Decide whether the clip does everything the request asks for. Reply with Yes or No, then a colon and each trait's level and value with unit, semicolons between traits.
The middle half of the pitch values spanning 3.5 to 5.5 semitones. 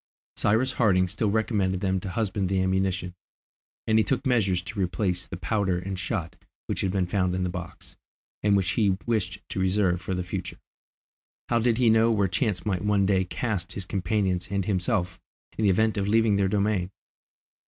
No: average, 2.8 semitones